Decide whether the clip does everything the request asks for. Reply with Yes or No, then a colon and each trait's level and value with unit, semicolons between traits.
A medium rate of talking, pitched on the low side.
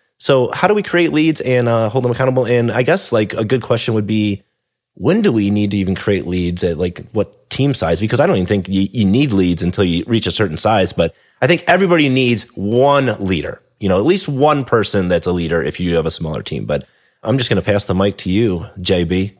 No: fast, 250 wpm; low, 105 Hz